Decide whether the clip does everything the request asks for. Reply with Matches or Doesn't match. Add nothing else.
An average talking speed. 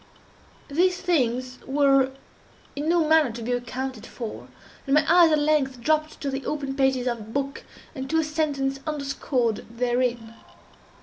Matches